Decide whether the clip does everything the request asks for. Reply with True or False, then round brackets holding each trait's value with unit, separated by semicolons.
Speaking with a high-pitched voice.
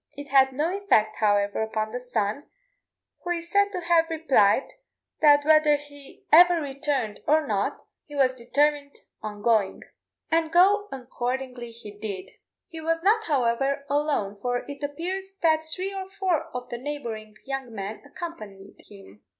True (280 Hz)